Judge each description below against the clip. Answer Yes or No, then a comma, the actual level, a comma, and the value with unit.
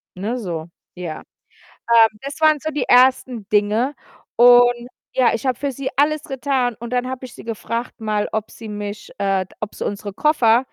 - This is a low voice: No, high, 235 Hz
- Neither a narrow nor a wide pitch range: Yes, average, 3.6 semitones